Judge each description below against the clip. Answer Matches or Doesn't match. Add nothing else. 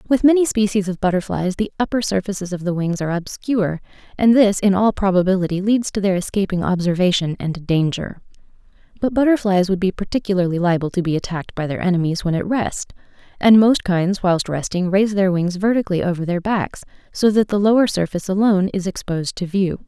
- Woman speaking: Matches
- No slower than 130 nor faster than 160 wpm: Doesn't match